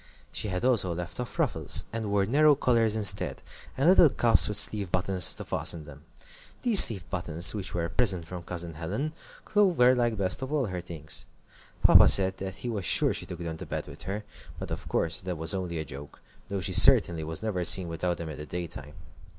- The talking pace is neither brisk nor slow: No, fast, 215 wpm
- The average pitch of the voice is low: Yes, very low, 95 Hz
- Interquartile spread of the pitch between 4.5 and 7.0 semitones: Yes, average, 4.8 semitones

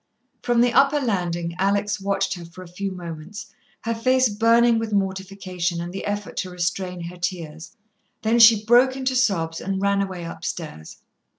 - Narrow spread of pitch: No, average, 4.4 semitones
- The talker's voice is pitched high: Yes, high, 195 Hz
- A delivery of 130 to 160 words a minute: No, average, 170 wpm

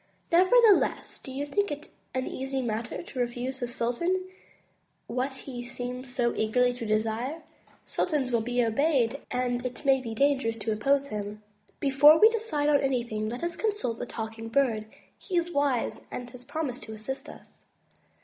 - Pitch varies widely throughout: No, average, 3.6 semitones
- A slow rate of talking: No, average, 170 wpm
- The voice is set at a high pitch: Yes, very high, 255 Hz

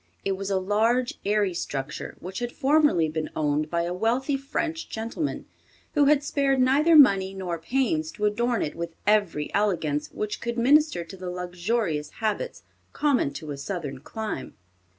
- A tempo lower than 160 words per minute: No, average, 165 wpm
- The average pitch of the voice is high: Yes, high, 210 Hz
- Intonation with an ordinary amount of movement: No, wide, 7.6 semitones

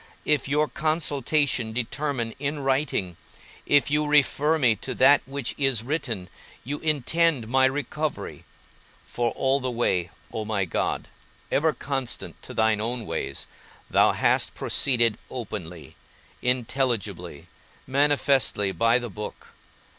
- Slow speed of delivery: Yes, slow, 125 wpm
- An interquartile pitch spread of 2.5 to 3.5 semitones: No, average, 4.2 semitones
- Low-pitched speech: Yes, low, 130 Hz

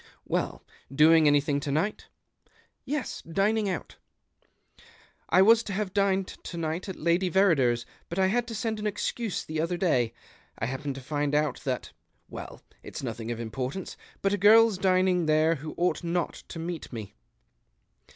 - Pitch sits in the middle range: Yes, medium, 170 Hz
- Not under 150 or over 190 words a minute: Yes, average, 180 wpm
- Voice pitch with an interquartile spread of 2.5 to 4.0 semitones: No, average, 5.1 semitones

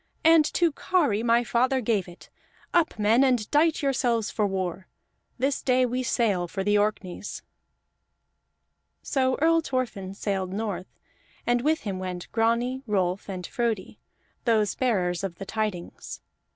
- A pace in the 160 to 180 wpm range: No, average, 140 wpm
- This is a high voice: Yes, high, 225 Hz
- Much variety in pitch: No, average, 4.9 semitones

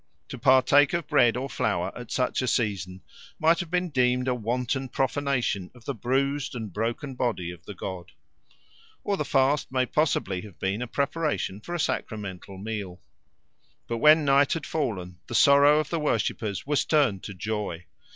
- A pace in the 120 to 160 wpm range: No, average, 175 wpm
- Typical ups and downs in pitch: No, wide, 5.8 semitones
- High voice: No, low, 125 Hz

